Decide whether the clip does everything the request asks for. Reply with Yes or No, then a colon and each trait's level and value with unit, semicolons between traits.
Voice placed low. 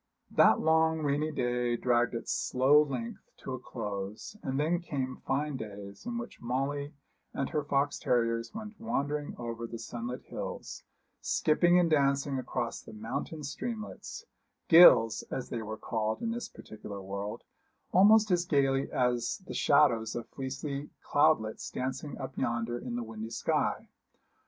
Yes: low, 130 Hz